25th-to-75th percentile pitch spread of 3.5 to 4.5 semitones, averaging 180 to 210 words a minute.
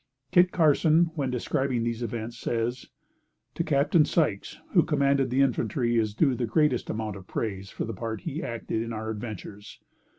No: average, 4.1 semitones; average, 170 wpm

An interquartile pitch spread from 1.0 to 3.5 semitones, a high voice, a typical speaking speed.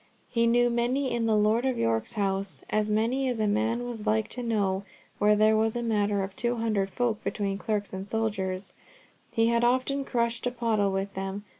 Yes: average, 2.8 semitones; high, 220 Hz; average, 195 wpm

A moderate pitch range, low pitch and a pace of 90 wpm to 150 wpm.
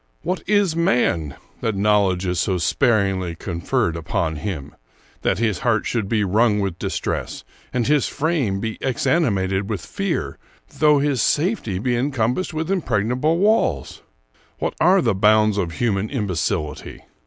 No: wide, 7.0 semitones; low, 110 Hz; average, 140 wpm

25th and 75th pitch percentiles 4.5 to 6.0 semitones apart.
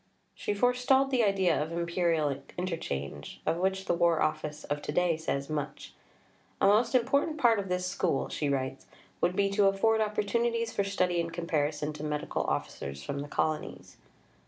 Yes: wide, 5.4 semitones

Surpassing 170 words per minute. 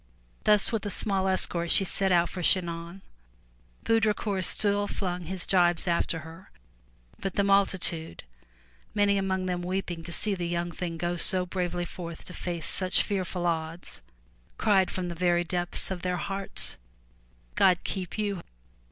No: average, 160 wpm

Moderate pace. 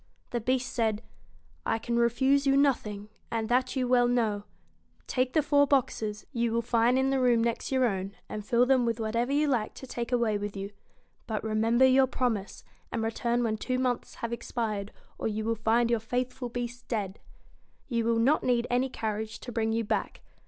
Yes: average, 195 wpm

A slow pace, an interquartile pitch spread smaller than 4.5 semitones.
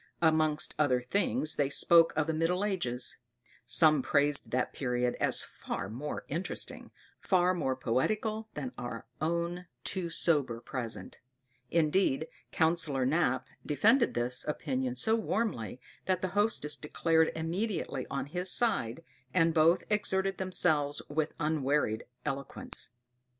No: slow, 125 wpm; average, 5.1 semitones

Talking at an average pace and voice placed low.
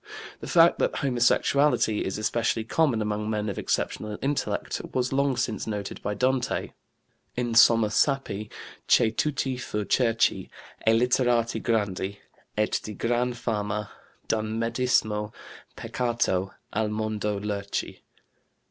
No: slow, 120 wpm; low, 115 Hz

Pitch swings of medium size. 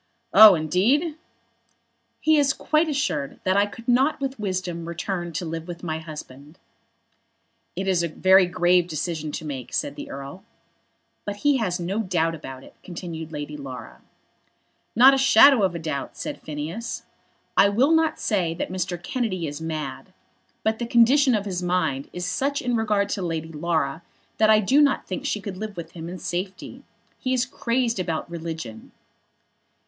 No: wide, 6.0 semitones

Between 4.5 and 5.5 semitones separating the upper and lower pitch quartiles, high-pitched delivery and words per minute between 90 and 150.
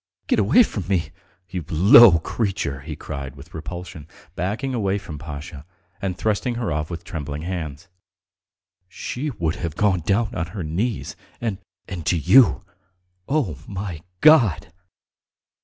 No: average, 5.1 semitones; very low, 90 Hz; average, 140 wpm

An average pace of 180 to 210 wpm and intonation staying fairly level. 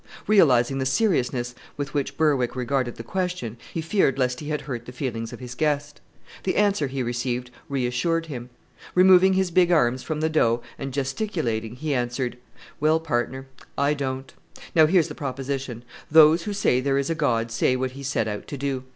No: average, 185 wpm; average, 4.1 semitones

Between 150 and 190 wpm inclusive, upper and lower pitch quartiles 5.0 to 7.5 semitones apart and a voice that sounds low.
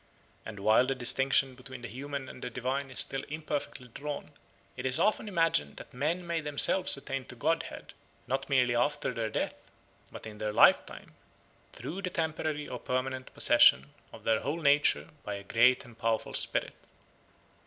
No: average, 170 wpm; average, 3.6 semitones; low, 130 Hz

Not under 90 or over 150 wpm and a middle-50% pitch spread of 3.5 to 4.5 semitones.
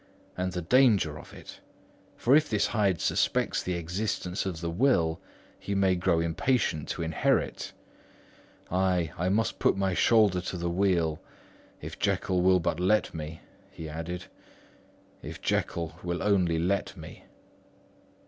No: average, 140 wpm; average, 2.9 semitones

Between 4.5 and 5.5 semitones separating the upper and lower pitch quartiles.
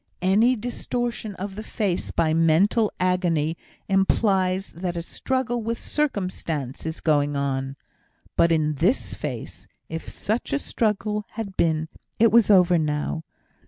Yes: average, 5.1 semitones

